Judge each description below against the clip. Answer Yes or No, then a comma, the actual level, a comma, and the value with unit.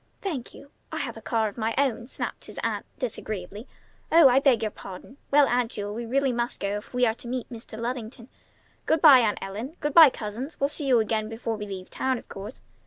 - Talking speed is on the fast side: Yes, fast, 230 wpm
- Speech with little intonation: No, average, 3.7 semitones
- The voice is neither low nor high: No, high, 235 Hz